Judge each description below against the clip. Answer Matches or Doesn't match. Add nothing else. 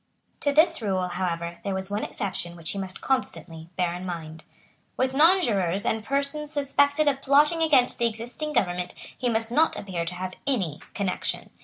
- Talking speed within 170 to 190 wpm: Matches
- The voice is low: Doesn't match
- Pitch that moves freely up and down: Matches